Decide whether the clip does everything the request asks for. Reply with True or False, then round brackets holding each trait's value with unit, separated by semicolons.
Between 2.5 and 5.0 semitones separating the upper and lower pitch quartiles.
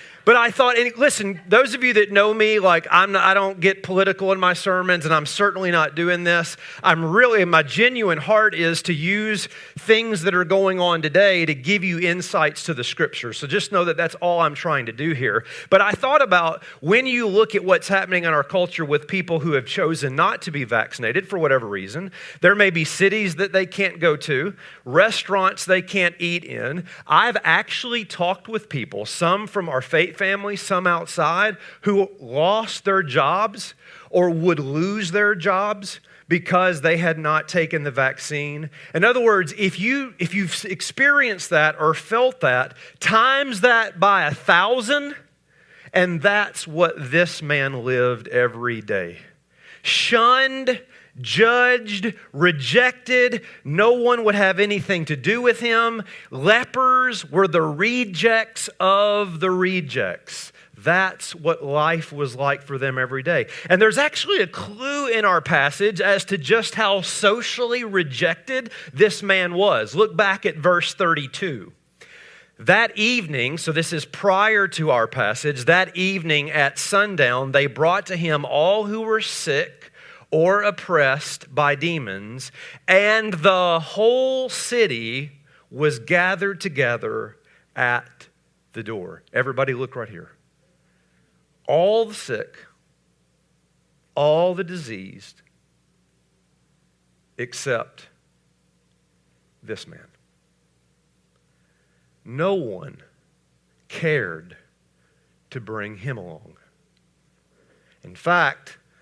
False (5.4 semitones)